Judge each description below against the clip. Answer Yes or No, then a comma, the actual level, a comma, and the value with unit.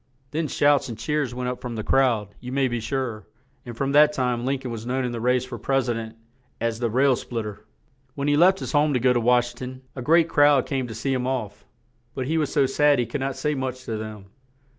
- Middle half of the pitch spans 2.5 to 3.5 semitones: Yes, average, 2.8 semitones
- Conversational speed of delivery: No, fast, 260 wpm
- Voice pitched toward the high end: No, low, 125 Hz